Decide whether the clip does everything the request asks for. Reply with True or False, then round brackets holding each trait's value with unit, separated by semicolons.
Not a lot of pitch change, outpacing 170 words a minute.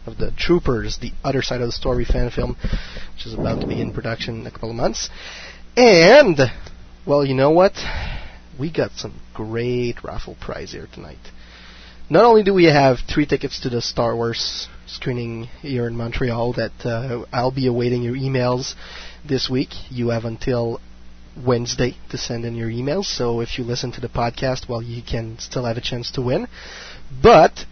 True (2.2 semitones; 185 wpm)